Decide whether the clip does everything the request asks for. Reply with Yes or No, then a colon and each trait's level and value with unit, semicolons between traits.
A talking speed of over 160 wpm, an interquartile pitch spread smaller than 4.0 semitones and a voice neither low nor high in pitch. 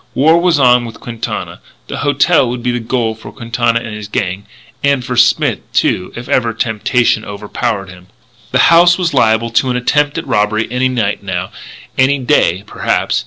No: average, 180 wpm; average, 3.4 semitones; low, 120 Hz